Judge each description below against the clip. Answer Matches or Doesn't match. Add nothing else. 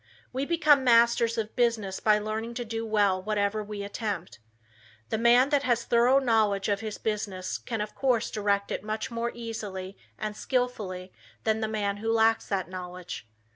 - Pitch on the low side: Doesn't match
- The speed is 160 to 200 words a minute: Matches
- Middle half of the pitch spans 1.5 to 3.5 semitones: Matches